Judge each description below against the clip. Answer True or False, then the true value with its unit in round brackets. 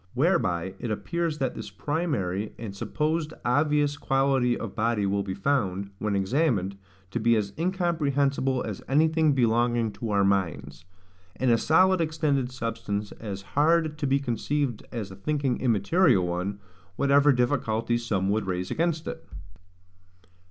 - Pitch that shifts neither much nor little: False (6.5 semitones)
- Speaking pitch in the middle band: False (125 Hz)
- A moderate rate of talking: True (145 wpm)